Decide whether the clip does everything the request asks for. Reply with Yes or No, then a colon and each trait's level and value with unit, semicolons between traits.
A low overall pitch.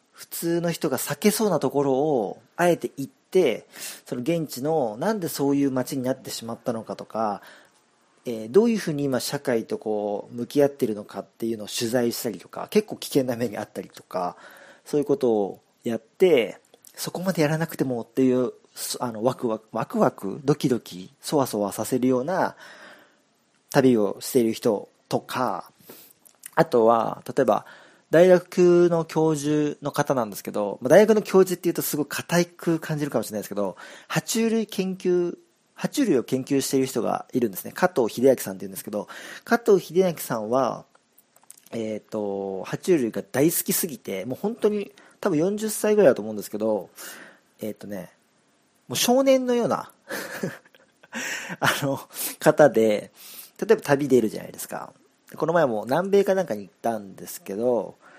No: medium, 145 Hz